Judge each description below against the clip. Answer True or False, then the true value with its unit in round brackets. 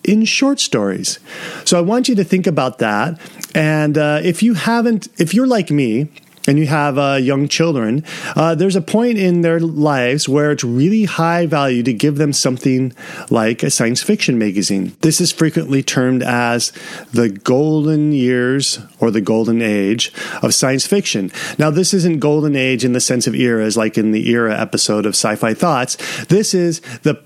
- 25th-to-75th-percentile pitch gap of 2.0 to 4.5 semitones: False (5.6 semitones)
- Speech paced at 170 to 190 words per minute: True (185 wpm)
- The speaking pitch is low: False (150 Hz)